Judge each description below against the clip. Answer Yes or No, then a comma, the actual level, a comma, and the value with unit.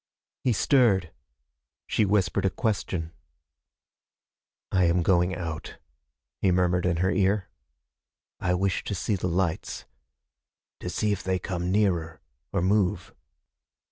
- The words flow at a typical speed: No, slow, 125 wpm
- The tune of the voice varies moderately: No, narrow, 2.3 semitones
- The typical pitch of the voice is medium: No, very low, 95 Hz